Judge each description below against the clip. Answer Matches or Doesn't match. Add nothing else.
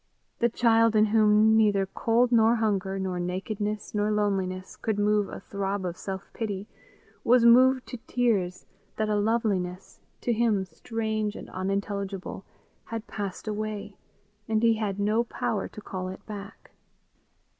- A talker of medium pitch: Doesn't match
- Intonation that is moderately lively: Doesn't match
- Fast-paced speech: Doesn't match